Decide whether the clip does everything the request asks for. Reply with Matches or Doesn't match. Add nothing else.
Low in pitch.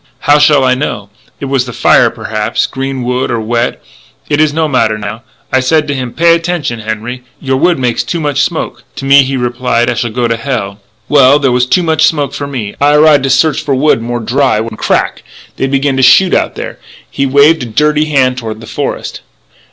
Matches